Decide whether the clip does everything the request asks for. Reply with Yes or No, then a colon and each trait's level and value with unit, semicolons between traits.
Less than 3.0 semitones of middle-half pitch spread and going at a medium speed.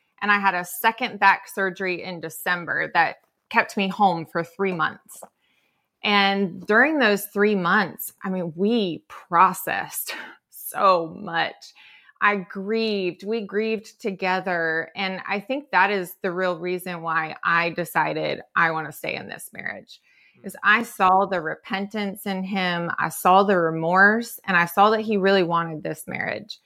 Yes: narrow, 2.5 semitones; average, 160 wpm